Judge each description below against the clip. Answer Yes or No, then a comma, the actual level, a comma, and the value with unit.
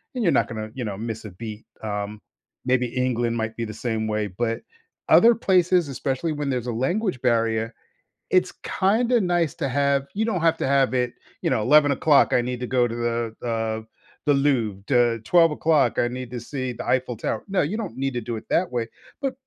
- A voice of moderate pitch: No, low, 125 Hz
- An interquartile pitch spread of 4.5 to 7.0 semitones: Yes, average, 4.8 semitones